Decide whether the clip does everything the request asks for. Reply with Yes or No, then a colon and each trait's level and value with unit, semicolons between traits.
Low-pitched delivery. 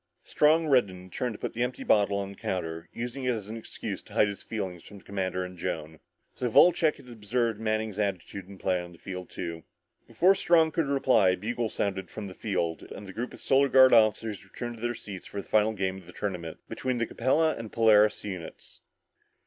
Yes: low, 105 Hz